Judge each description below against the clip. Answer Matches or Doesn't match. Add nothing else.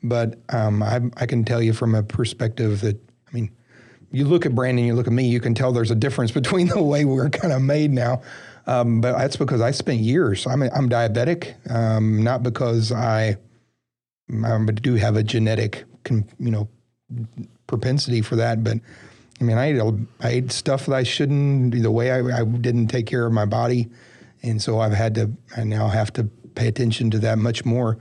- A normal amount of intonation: Doesn't match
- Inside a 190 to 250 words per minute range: Matches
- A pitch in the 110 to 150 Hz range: Matches